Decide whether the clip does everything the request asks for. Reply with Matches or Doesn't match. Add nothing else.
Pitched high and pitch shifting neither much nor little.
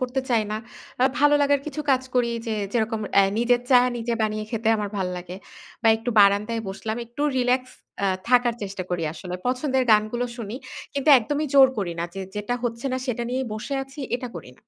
Matches